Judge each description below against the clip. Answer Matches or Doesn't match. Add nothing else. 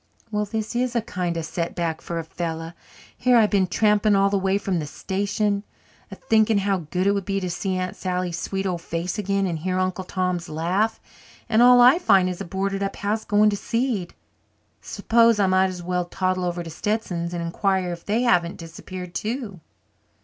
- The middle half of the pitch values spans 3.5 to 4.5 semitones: Doesn't match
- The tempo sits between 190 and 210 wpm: Matches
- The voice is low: Doesn't match